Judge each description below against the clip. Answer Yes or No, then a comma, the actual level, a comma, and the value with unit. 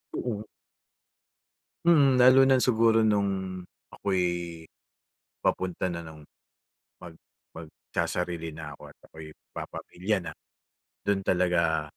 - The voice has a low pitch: Yes, very low, 90 Hz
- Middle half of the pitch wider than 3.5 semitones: Yes, average, 4.7 semitones